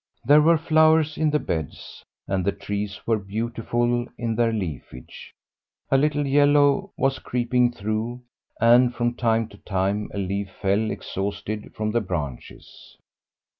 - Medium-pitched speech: No, low, 115 Hz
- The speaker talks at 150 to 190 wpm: No, average, 140 wpm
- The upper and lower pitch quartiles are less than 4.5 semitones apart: No, average, 5.0 semitones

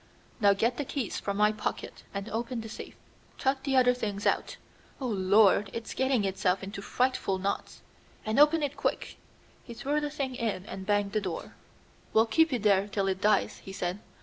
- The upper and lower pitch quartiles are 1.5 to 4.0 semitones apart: No, average, 4.4 semitones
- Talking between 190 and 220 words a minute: Yes, average, 195 wpm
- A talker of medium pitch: No, high, 215 Hz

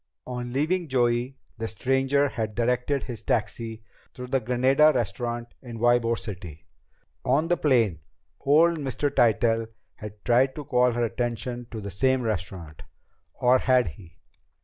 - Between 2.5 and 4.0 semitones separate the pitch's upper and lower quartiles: Yes, average, 2.8 semitones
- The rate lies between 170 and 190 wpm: No, average, 145 wpm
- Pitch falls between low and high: No, low, 120 Hz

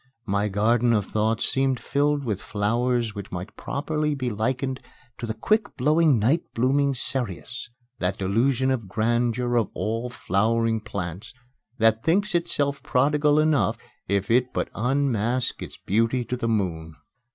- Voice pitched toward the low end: Yes, low, 120 Hz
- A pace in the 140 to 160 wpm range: Yes, average, 145 wpm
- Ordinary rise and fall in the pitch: Yes, average, 4.0 semitones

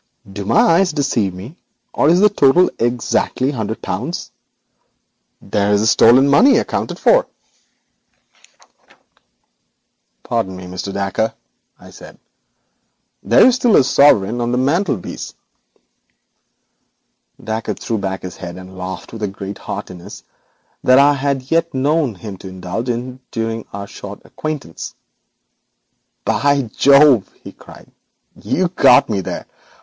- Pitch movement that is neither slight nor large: No, wide, 6.2 semitones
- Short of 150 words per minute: Yes, slow, 135 wpm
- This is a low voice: Yes, low, 120 Hz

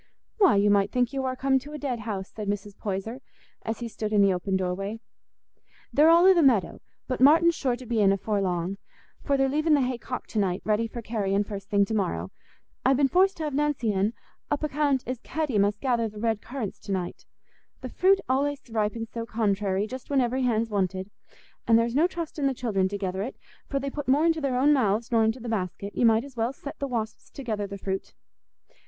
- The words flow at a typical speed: No, fast, 230 wpm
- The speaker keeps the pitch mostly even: No, average, 5.1 semitones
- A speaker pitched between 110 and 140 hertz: No, high, 230 Hz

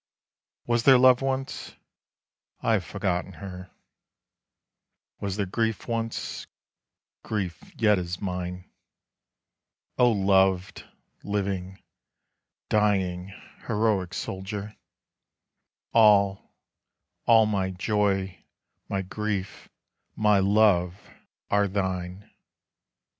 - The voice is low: Yes, low, 100 Hz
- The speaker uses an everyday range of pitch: No, narrow, 2.3 semitones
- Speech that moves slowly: Yes, slow, 85 wpm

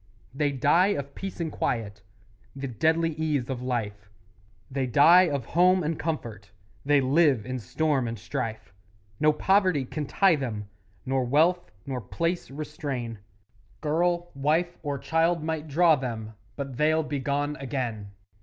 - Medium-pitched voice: Yes, medium, 145 Hz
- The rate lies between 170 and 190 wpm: No, average, 145 wpm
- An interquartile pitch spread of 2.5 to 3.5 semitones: No, average, 4.2 semitones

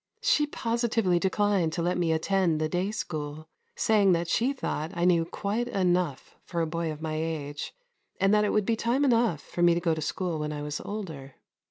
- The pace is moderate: No, fast, 210 wpm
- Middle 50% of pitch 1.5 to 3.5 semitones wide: No, average, 4.8 semitones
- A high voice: No, medium, 175 Hz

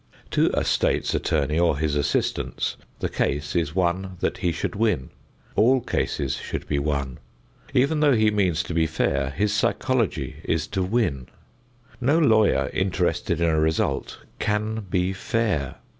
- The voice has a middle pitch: No, very low, 90 Hz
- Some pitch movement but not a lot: No, wide, 6.1 semitones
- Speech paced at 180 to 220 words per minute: No, average, 155 wpm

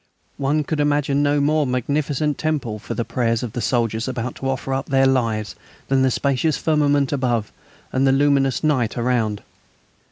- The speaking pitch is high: No, low, 135 Hz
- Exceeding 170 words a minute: No, average, 165 wpm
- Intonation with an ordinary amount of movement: Yes, average, 3.0 semitones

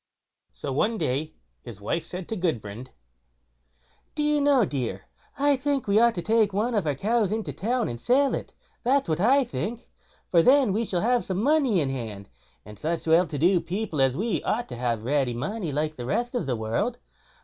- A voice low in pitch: No, high, 190 Hz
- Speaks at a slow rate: No, fast, 205 wpm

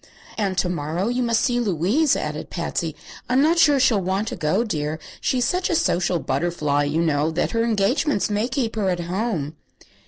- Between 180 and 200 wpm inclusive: Yes, average, 190 wpm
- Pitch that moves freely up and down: Yes, wide, 6.3 semitones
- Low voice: No, high, 195 Hz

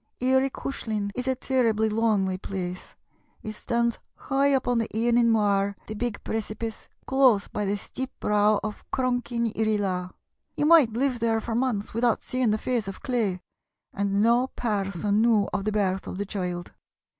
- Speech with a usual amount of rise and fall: Yes, average, 3.3 semitones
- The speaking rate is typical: Yes, average, 175 wpm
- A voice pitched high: Yes, high, 220 Hz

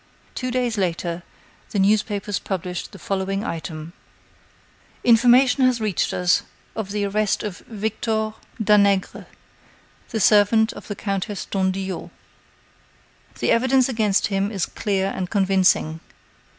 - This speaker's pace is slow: Yes, slow, 120 wpm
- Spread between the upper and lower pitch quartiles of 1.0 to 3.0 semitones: Yes, narrow, 2.5 semitones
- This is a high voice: Yes, high, 200 Hz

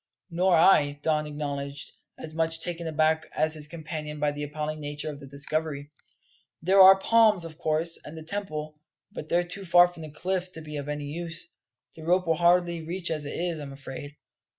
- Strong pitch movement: No, narrow, 2.6 semitones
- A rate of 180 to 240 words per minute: Yes, average, 200 wpm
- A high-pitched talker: No, medium, 160 Hz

